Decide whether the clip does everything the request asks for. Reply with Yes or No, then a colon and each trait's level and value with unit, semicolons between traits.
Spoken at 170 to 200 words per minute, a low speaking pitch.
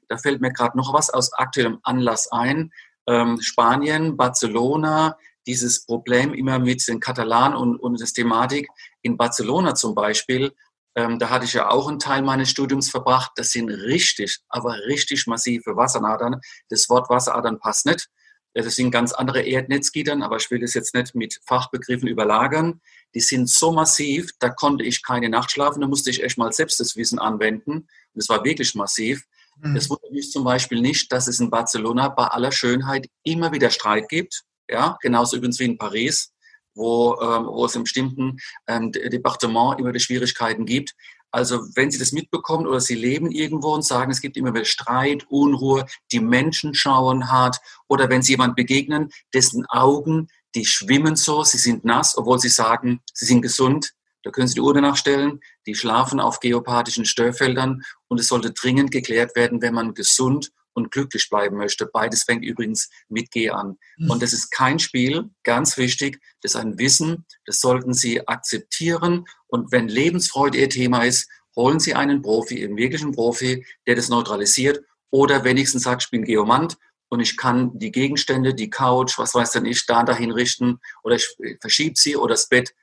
Yes: average, 180 wpm; low, 125 Hz